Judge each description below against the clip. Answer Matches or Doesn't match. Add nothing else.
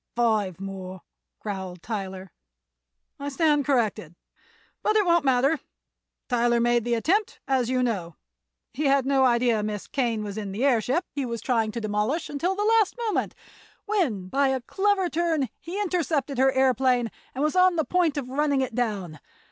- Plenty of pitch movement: Matches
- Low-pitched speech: Doesn't match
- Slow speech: Doesn't match